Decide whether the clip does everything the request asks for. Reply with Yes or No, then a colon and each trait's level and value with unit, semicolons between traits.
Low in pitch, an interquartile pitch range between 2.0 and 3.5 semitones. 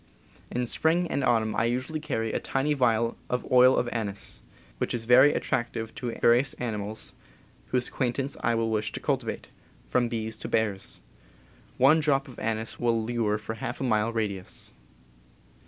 Yes: low, 120 Hz; narrow, 2.5 semitones